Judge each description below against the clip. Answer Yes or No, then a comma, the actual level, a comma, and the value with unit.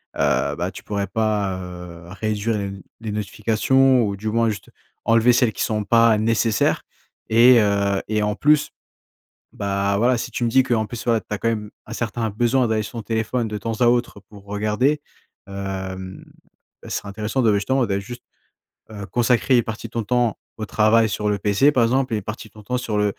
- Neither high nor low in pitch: No, low, 110 Hz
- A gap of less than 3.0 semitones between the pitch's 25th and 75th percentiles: Yes, narrow, 2.5 semitones